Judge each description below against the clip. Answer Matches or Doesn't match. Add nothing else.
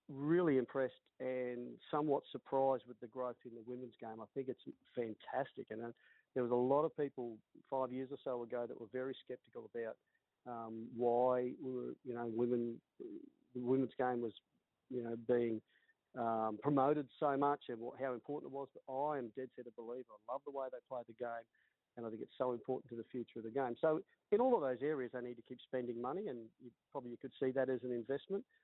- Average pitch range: Doesn't match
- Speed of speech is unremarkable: Doesn't match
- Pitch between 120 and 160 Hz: Matches